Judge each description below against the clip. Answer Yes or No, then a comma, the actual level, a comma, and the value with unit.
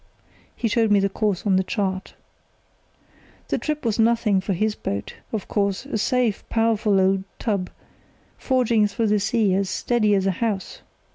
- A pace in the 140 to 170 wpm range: Yes, average, 165 wpm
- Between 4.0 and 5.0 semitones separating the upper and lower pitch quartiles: No, average, 2.8 semitones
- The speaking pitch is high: Yes, high, 210 Hz